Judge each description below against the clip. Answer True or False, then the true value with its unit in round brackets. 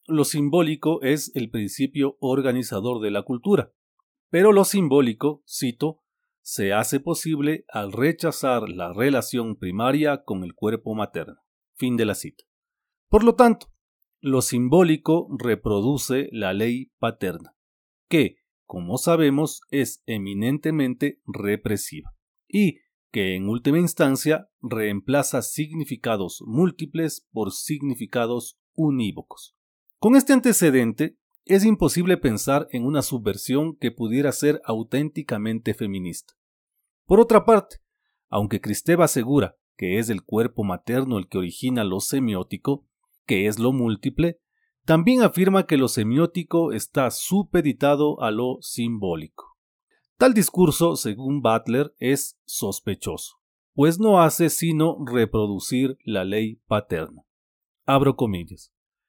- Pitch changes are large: True (6.5 semitones)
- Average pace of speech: False (115 wpm)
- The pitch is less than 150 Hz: True (140 Hz)